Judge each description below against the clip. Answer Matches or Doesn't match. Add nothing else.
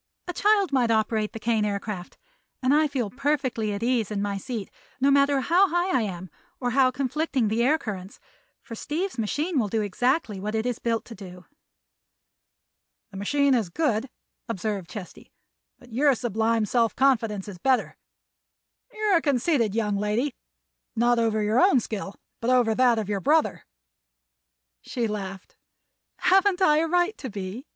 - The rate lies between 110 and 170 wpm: Matches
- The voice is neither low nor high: Doesn't match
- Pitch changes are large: Doesn't match